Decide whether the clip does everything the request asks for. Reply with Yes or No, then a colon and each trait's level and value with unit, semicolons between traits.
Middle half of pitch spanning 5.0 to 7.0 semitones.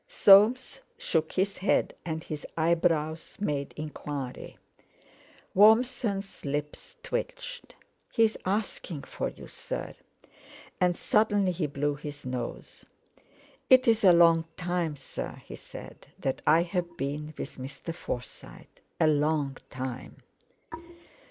Yes: average, 5.3 semitones